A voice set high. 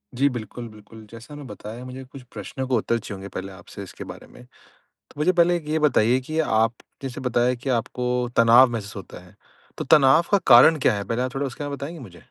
No: low, 125 Hz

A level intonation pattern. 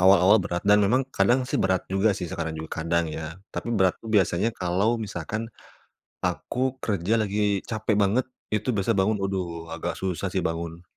No: average, 3.9 semitones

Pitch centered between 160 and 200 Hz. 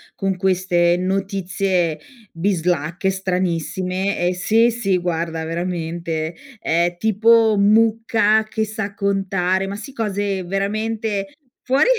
Yes: high, 190 Hz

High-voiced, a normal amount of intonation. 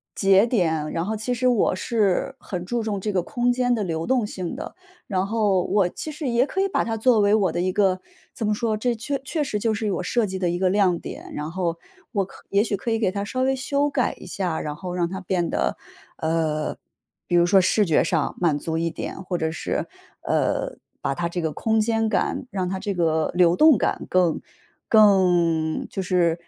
Yes: high, 195 Hz; average, 4.4 semitones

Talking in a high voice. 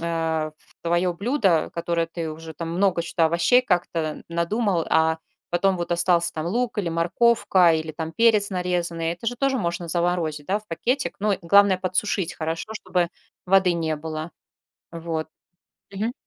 No: medium, 170 Hz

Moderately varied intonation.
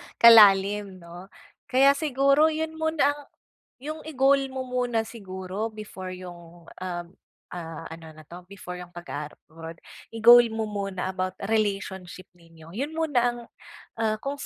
No: wide, 6.3 semitones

